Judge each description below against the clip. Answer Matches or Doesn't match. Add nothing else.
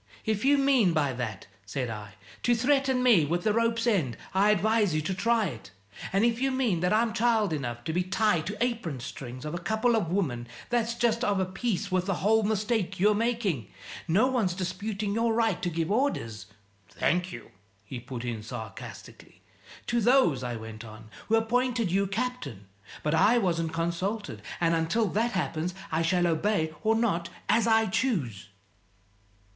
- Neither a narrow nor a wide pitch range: Doesn't match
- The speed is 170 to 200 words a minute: Matches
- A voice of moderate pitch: Doesn't match